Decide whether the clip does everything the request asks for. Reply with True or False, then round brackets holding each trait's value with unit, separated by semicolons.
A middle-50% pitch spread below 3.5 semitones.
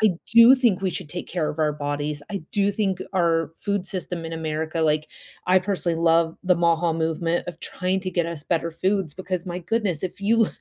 True (2.8 semitones)